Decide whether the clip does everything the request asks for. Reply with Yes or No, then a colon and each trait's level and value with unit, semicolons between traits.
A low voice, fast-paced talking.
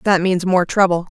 No: medium, 185 Hz; fast, 210 wpm